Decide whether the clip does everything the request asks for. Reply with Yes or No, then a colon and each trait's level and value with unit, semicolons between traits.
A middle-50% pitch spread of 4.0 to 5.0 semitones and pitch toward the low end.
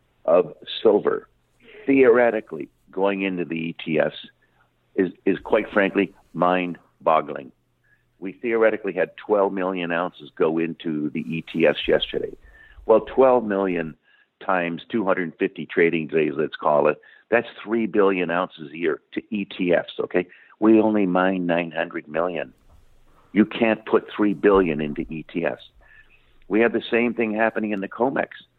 Yes: average, 4.5 semitones; very low, 95 Hz